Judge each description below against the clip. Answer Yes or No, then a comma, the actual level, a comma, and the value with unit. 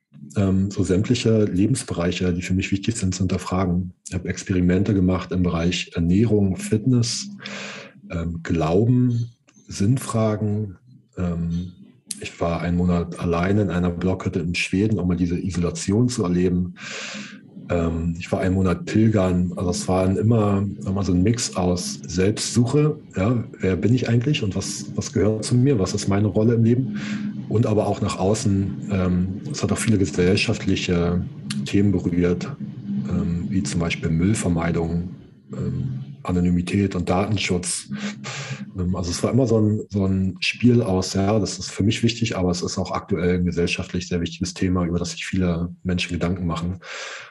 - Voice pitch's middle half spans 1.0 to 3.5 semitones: Yes, average, 3.2 semitones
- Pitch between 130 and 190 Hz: No, very low, 95 Hz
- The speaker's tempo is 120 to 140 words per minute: No, average, 160 wpm